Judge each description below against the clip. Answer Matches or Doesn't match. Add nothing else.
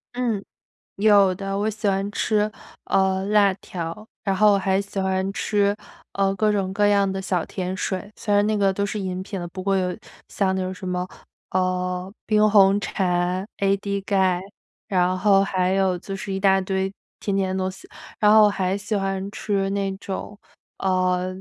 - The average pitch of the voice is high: Matches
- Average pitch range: Doesn't match